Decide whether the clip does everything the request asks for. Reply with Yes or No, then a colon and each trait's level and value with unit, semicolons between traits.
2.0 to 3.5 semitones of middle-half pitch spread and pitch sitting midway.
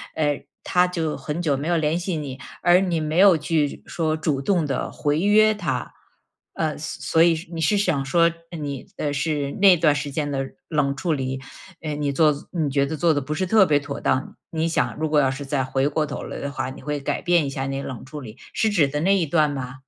Yes: average, 3.2 semitones; medium, 150 Hz